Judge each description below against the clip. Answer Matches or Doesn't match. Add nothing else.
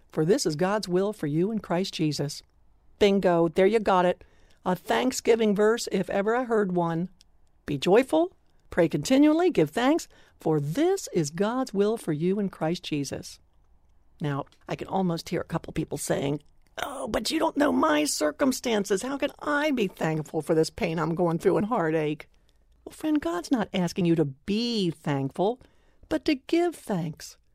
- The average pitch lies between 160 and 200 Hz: Matches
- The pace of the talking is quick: Doesn't match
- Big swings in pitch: Matches